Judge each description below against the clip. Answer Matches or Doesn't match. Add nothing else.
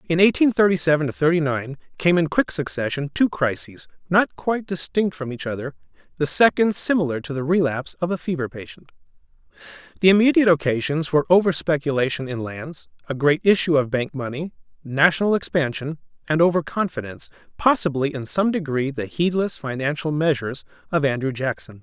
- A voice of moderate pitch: Matches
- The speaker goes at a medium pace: Matches